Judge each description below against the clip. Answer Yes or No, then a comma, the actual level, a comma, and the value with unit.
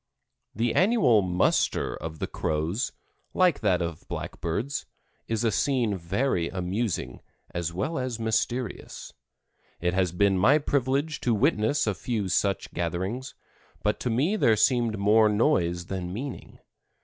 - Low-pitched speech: Yes, low, 105 Hz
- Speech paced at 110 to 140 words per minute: Yes, slow, 135 wpm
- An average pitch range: No, wide, 5.8 semitones